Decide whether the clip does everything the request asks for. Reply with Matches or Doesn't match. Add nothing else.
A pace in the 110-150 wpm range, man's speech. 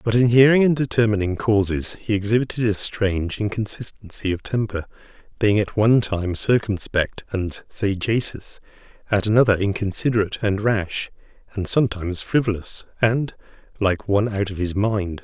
Matches